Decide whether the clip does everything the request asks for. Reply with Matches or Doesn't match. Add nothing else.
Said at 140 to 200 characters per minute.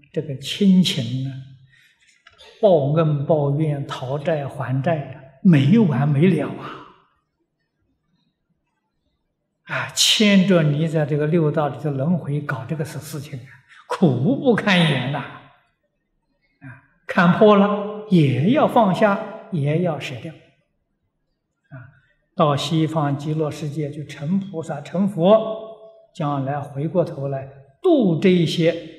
Matches